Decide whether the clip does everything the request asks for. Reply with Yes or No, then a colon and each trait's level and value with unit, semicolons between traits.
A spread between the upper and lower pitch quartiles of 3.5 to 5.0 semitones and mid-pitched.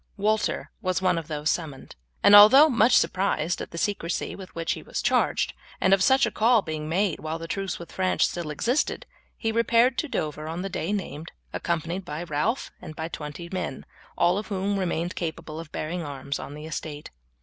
Yes: average, 4.2 semitones; medium, 175 Hz